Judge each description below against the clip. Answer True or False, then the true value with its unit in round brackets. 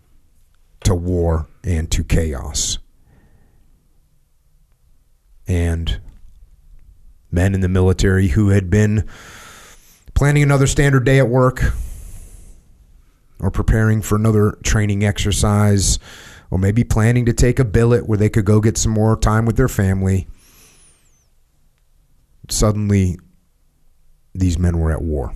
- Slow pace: True (115 wpm)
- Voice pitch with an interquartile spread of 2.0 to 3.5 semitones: False (4.8 semitones)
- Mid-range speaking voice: False (95 Hz)